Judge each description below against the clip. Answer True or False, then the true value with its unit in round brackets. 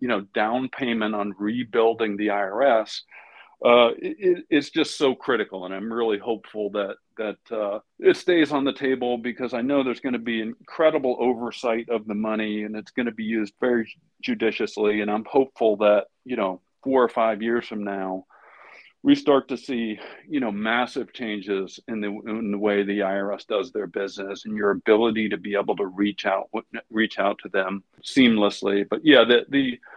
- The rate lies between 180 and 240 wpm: True (185 wpm)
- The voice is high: False (115 Hz)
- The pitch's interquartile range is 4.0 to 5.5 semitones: False (3.3 semitones)